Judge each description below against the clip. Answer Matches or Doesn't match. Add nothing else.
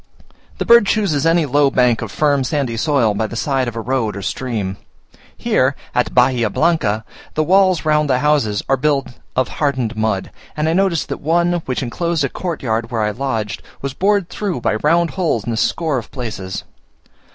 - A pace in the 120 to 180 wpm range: Doesn't match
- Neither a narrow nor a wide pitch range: Doesn't match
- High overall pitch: Doesn't match